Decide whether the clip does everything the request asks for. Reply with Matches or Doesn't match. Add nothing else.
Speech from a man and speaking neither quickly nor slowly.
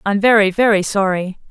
Doesn't match